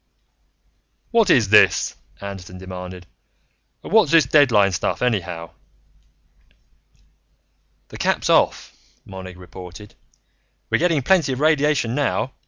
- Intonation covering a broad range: Yes, wide, 8.2 semitones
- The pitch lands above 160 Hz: No, low, 110 Hz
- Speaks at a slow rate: Yes, slow, 105 wpm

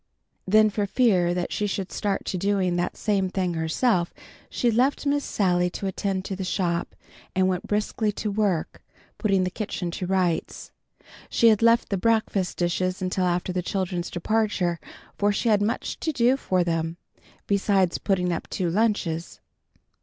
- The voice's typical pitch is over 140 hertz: Yes, high, 190 Hz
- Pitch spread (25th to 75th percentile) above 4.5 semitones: No, average, 3.0 semitones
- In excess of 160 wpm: Yes, average, 170 wpm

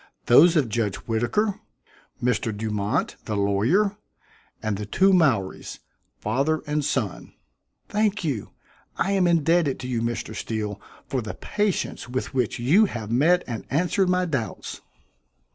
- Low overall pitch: Yes, low, 130 Hz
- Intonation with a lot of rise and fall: Yes, wide, 8.2 semitones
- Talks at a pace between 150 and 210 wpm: No, average, 140 wpm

